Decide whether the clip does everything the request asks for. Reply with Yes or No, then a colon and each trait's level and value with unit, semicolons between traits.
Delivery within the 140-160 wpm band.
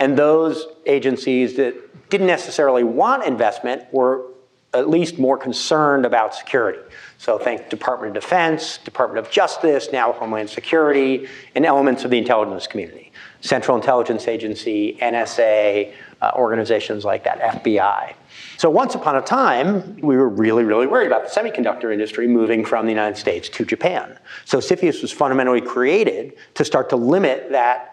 Yes: average, 155 wpm